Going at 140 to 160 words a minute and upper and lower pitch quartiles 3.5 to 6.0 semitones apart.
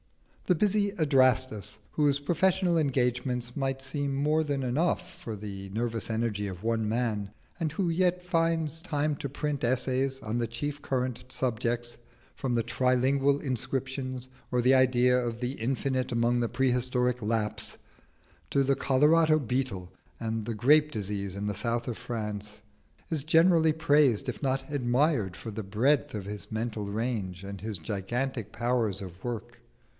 Yes: average, 155 wpm; average, 4.1 semitones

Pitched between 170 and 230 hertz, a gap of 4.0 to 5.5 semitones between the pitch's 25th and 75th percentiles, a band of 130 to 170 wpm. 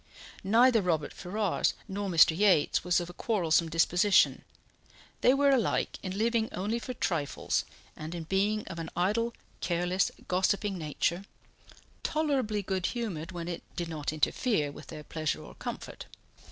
Yes: medium, 185 Hz; average, 4.3 semitones; average, 150 wpm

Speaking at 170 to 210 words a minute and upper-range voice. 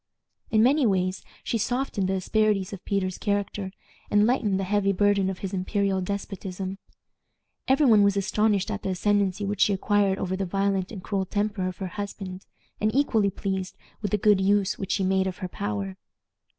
Yes: average, 185 wpm; high, 195 Hz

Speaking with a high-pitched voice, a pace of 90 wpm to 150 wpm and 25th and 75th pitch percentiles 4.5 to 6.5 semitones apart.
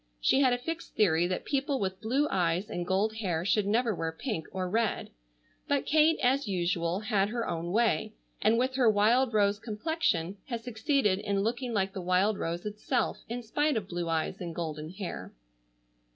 No: high, 210 Hz; average, 185 wpm; average, 5.0 semitones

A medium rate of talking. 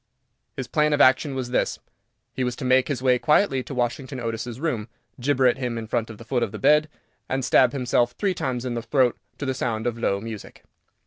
No: fast, 215 wpm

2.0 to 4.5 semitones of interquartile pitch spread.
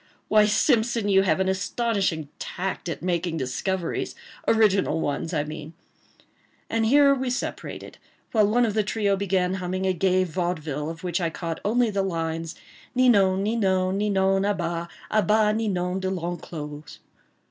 Yes: average, 3.7 semitones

